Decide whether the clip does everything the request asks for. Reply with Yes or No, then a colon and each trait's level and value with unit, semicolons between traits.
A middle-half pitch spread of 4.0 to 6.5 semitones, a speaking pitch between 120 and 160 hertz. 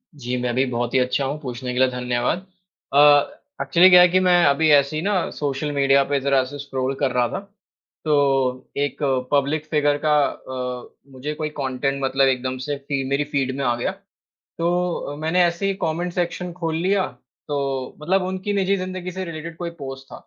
Yes: average, 4.5 semitones; medium, 140 Hz